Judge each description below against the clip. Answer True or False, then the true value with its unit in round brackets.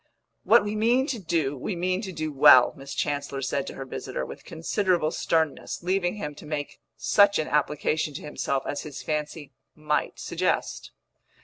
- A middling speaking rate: True (175 wpm)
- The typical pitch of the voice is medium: True (155 Hz)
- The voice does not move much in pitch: False (4.3 semitones)